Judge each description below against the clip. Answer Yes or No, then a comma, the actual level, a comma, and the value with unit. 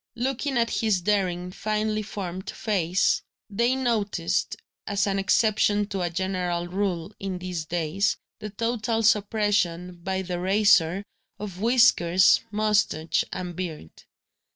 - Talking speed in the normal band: No, slow, 125 wpm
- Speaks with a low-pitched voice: No, high, 195 Hz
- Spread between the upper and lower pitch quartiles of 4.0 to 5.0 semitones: No, average, 3.2 semitones